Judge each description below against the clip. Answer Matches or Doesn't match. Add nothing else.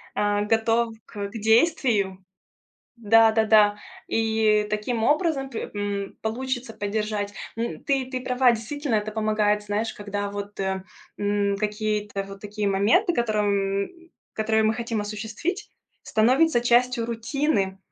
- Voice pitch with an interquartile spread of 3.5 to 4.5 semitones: Doesn't match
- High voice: Matches